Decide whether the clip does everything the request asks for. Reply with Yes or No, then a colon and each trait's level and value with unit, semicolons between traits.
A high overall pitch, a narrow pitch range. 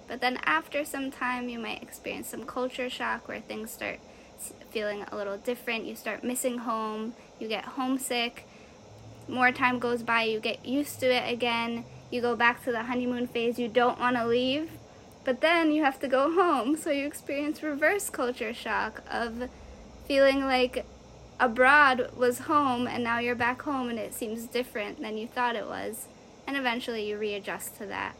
Yes: high, 245 Hz; narrow, 2.3 semitones